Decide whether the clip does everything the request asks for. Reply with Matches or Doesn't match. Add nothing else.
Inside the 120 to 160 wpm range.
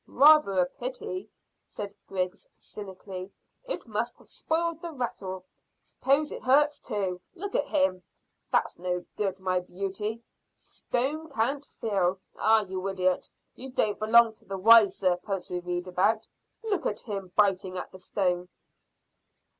Matches